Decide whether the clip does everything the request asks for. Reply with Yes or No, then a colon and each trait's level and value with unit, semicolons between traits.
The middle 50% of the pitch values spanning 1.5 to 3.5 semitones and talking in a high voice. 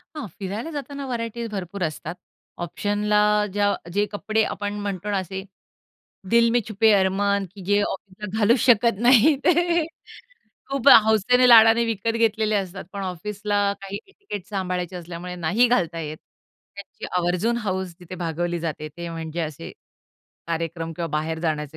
No: average, 4.4 semitones; high, 200 Hz